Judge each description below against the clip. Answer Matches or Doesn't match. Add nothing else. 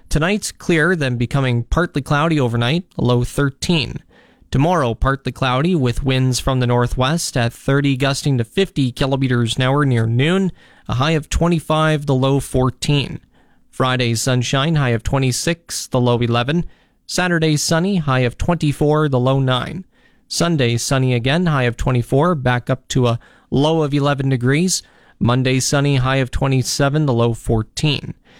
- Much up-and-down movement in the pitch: Doesn't match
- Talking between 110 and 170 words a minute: Matches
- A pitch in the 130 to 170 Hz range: Matches